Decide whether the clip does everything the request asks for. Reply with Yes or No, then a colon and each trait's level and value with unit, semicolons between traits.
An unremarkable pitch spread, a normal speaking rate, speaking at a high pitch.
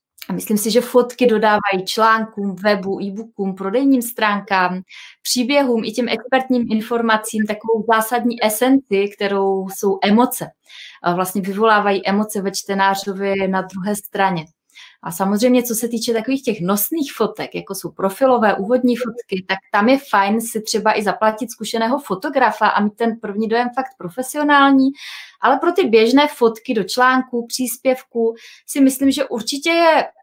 Yes: average, 3.9 semitones; average, 150 wpm; high, 225 Hz